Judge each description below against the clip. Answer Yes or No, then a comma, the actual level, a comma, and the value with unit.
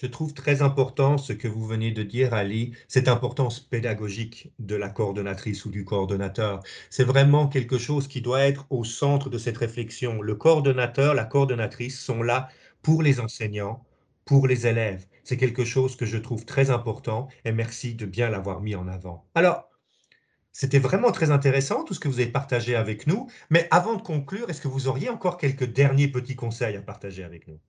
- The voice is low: Yes, low, 125 Hz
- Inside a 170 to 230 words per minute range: Yes, average, 195 wpm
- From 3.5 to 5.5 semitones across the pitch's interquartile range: Yes, average, 3.8 semitones